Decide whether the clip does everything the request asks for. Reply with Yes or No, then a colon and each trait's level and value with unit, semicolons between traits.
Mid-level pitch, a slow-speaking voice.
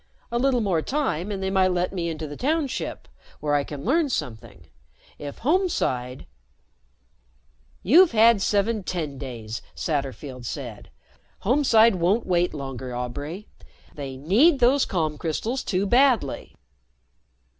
Yes: medium, 175 Hz; slow, 130 wpm